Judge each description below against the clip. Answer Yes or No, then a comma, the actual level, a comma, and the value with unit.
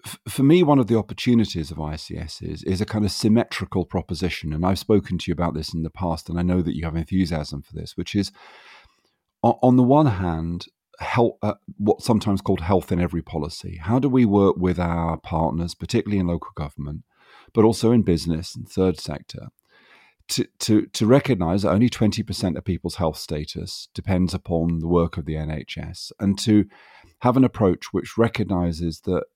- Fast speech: No, average, 190 wpm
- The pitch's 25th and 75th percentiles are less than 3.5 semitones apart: No, average, 4.3 semitones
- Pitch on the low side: Yes, very low, 95 Hz